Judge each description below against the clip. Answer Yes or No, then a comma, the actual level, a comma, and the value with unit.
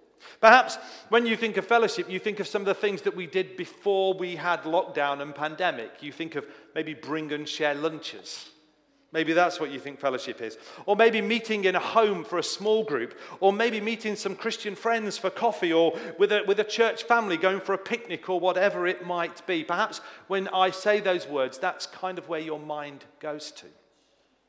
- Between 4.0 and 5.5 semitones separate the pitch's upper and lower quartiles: Yes, average, 4.5 semitones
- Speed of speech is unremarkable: No, fast, 210 wpm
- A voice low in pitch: No, medium, 185 Hz